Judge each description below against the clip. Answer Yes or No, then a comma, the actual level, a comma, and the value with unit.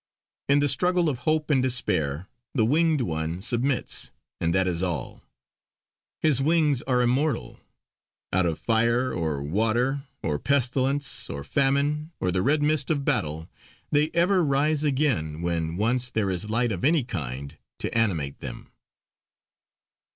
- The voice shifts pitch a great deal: Yes, wide, 8.7 semitones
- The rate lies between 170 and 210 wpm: No, average, 145 wpm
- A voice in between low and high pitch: No, low, 125 Hz